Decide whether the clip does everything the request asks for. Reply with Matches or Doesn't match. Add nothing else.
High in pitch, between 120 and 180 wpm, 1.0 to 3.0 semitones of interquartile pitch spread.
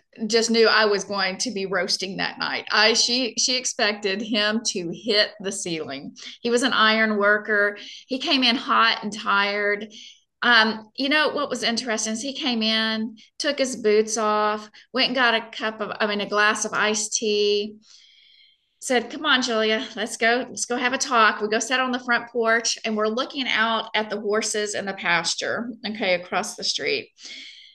Doesn't match